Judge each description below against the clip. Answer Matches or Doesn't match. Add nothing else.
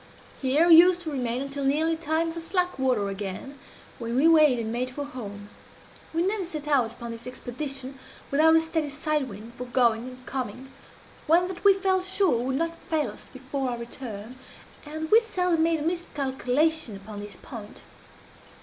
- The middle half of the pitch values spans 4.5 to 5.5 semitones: Matches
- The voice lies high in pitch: Matches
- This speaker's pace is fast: Doesn't match